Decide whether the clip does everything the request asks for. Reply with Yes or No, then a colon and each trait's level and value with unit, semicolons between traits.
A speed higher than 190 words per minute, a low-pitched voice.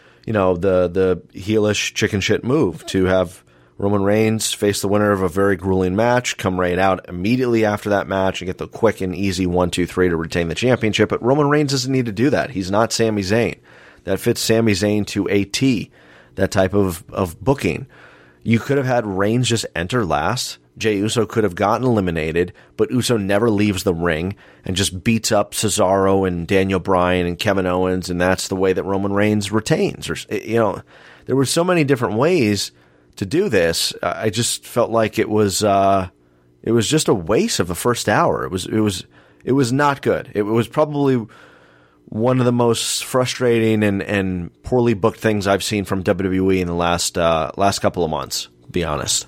Yes: average, 200 wpm; low, 100 Hz